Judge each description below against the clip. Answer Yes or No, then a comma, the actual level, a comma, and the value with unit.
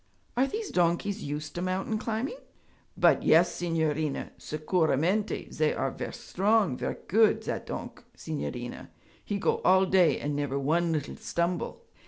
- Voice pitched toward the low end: No, medium, 175 Hz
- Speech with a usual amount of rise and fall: Yes, average, 4.9 semitones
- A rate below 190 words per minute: Yes, average, 145 wpm